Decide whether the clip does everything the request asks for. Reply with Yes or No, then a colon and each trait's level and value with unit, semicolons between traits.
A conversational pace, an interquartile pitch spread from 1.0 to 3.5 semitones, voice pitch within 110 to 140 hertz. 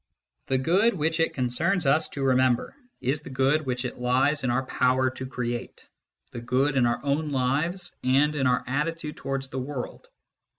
Yes: average, 180 wpm; average, 3.0 semitones; low, 135 Hz